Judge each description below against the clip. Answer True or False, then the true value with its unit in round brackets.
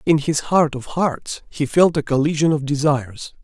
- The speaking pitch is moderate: True (150 Hz)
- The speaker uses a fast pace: False (190 wpm)